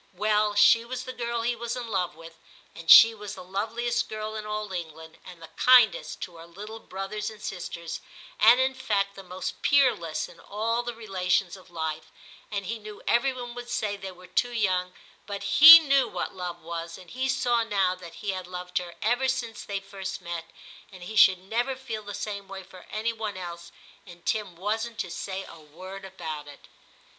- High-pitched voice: Yes, high, 200 Hz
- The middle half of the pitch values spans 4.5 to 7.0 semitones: No, average, 4.1 semitones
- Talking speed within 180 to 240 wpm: Yes, fast, 205 wpm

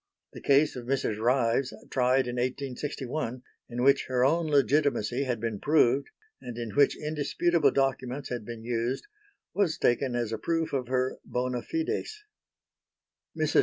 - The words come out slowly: No, average, 150 wpm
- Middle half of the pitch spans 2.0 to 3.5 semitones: Yes, average, 3.0 semitones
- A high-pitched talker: No, low, 130 Hz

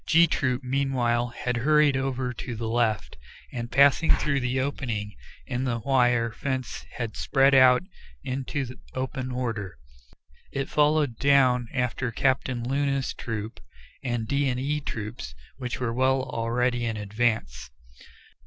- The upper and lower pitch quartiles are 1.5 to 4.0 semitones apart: Yes, narrow, 2.5 semitones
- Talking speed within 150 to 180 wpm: No, slow, 135 wpm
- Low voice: Yes, low, 125 Hz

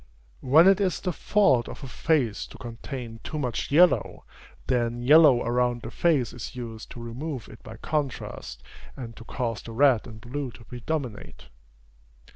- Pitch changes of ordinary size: Yes, average, 4.2 semitones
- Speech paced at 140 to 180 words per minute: Yes, average, 165 wpm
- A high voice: No, low, 125 Hz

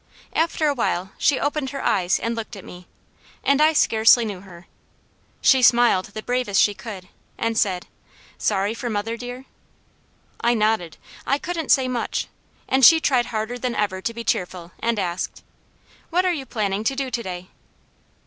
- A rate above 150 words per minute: Yes, average, 175 wpm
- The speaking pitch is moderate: No, high, 230 Hz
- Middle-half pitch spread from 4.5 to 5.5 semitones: Yes, average, 4.8 semitones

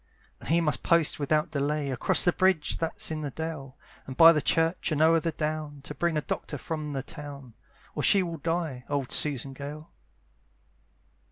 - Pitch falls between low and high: Yes, medium, 150 Hz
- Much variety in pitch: No, narrow, 2.5 semitones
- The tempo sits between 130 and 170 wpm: No, average, 185 wpm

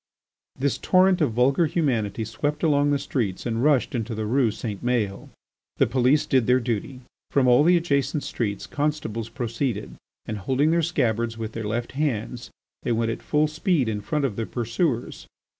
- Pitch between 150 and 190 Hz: No, low, 125 Hz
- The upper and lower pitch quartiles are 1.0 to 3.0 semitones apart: No, average, 4.3 semitones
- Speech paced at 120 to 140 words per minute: No, average, 175 wpm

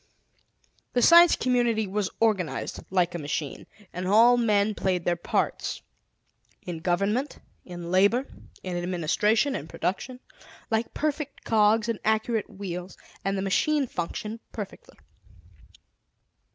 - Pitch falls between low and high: No, high, 205 Hz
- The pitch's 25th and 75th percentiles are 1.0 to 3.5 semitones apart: No, average, 4.4 semitones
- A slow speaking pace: Yes, slow, 120 wpm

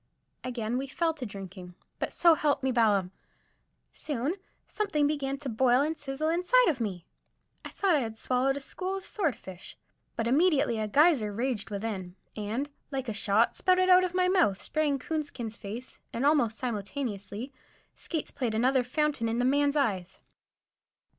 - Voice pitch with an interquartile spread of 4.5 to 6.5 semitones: Yes, wide, 5.5 semitones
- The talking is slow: No, average, 165 wpm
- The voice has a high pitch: Yes, very high, 260 Hz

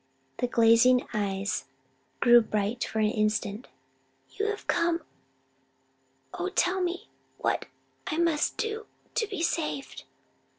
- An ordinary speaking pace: No, slow, 120 wpm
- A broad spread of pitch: Yes, wide, 8.5 semitones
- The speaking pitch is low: No, very high, 260 Hz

